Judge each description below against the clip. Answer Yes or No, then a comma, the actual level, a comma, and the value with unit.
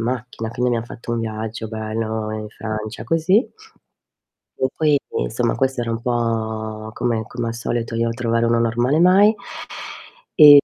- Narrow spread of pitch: Yes, narrow, 1.9 semitones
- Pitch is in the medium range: No, low, 115 Hz